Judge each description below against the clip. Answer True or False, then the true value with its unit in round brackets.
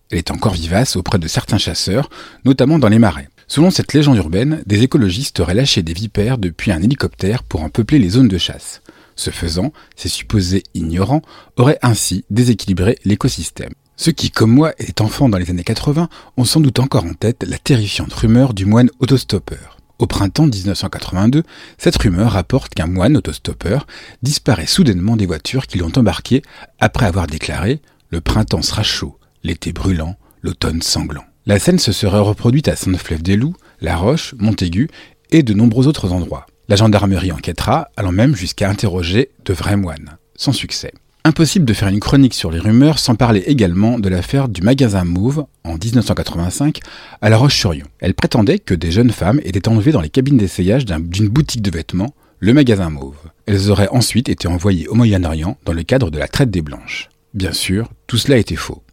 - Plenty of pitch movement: True (5.8 semitones)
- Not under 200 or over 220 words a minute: False (180 wpm)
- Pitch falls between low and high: False (105 Hz)